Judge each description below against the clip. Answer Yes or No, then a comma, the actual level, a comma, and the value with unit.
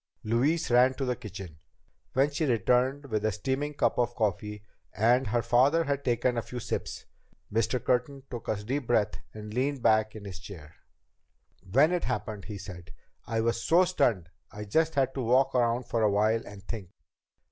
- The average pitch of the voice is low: Yes, low, 120 Hz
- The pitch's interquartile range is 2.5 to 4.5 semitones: Yes, average, 4.0 semitones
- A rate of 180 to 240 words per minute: Yes, average, 185 wpm